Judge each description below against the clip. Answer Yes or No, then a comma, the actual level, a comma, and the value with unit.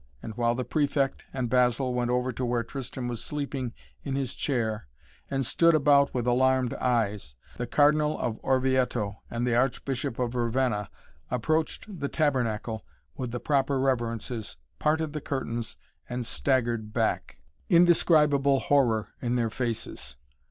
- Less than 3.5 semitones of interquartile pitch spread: Yes, average, 3.0 semitones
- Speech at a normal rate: Yes, average, 145 wpm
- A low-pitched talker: Yes, low, 125 Hz